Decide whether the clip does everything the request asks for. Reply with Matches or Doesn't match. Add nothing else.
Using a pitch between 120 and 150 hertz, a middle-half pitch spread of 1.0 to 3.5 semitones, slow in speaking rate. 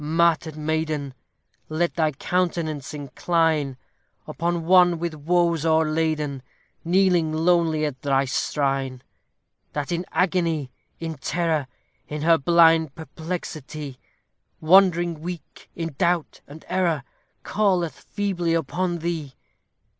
Doesn't match